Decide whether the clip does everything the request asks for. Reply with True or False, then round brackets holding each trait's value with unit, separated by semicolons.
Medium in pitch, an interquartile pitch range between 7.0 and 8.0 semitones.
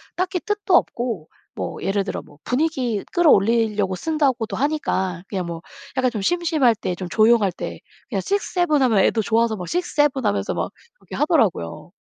False (235 Hz; 7.6 semitones)